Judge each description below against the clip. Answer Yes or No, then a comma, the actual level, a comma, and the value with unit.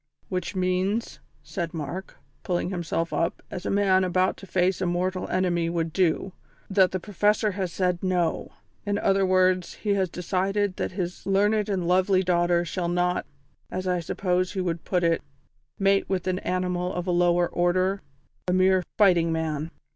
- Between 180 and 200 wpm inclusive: No, average, 170 wpm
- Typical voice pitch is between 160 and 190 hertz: Yes, medium, 185 Hz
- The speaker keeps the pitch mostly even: Yes, narrow, 1.5 semitones